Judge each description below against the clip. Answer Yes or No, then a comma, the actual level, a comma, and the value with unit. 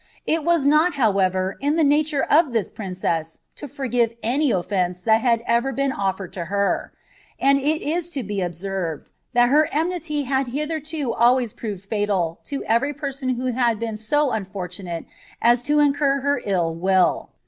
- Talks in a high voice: Yes, high, 240 Hz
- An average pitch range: No, wide, 6.6 semitones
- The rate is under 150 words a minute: No, average, 170 wpm